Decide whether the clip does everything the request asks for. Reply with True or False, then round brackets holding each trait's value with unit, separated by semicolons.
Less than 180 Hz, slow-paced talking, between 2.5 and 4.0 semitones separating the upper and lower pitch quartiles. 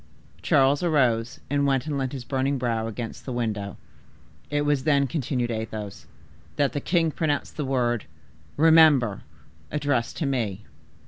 False (135 Hz; 145 wpm; 3.7 semitones)